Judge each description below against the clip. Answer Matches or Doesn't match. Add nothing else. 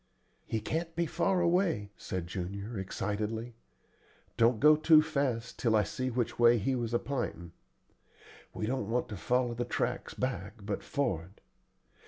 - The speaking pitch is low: Matches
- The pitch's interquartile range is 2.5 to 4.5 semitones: Doesn't match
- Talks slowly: Doesn't match